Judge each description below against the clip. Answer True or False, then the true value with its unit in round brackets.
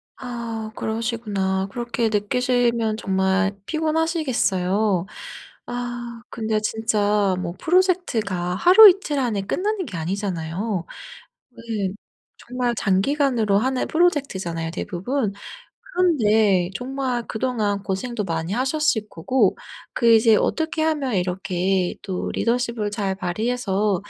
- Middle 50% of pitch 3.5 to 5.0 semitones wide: True (4.6 semitones)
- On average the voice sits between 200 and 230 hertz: True (220 Hz)